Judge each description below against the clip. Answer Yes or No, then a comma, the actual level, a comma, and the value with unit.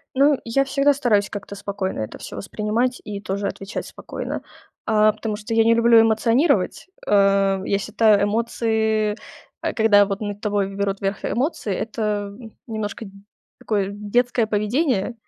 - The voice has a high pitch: Yes, high, 210 Hz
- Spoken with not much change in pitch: Yes, narrow, 2.3 semitones